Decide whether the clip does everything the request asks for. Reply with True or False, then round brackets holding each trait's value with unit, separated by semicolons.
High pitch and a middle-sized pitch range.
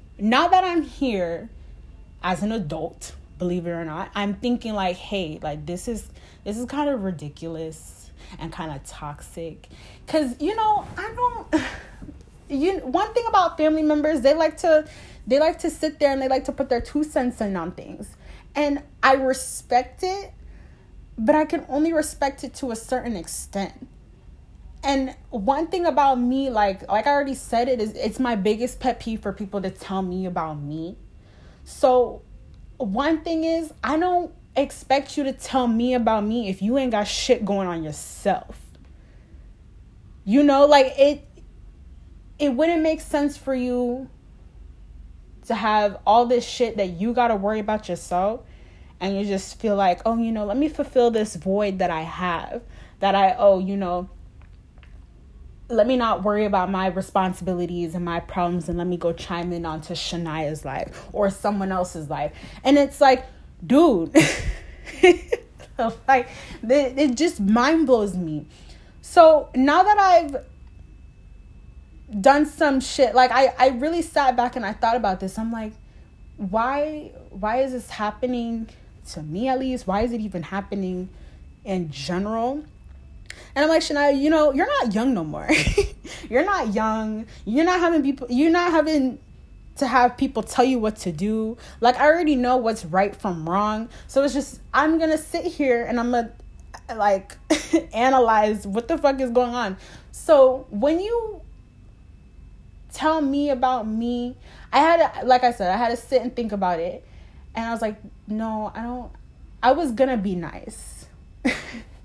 False (235 Hz; 6.6 semitones)